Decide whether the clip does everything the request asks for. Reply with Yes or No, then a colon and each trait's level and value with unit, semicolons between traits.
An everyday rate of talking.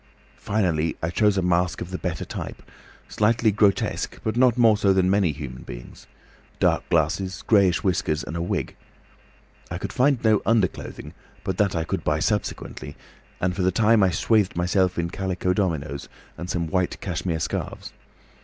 Yes: average, 170 wpm